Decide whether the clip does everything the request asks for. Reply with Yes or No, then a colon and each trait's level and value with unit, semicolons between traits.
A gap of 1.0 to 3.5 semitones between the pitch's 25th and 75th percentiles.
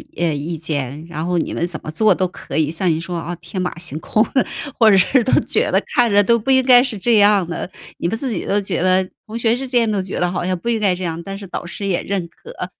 No: average, 4.4 semitones